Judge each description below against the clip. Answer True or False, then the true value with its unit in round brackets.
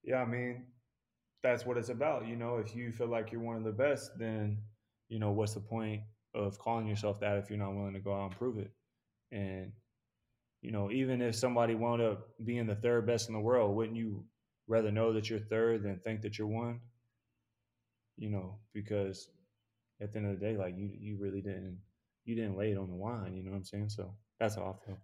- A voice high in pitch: False (110 Hz)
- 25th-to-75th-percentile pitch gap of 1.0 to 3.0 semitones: True (2.4 semitones)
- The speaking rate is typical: False (230 wpm)